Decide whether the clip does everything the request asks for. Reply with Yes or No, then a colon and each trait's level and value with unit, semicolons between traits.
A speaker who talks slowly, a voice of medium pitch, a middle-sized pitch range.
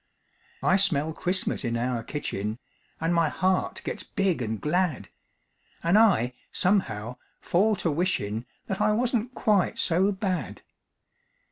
No: slow, 130 wpm; medium, 175 Hz; wide, 7.4 semitones